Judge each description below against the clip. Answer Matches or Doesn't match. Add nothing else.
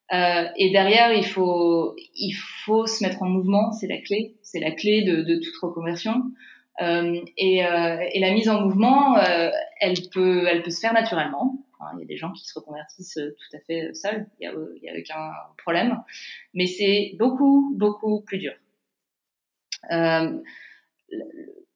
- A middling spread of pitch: Matches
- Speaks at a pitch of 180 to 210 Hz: Matches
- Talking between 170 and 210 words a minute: Doesn't match